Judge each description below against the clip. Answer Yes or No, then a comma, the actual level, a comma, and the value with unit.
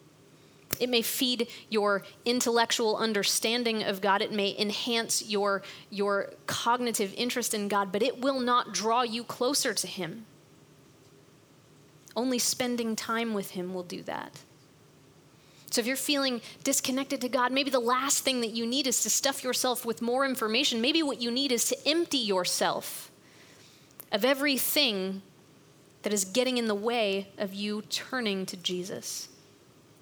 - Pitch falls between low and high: No, high, 230 Hz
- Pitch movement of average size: Yes, average, 3.9 semitones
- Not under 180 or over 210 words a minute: No, average, 150 wpm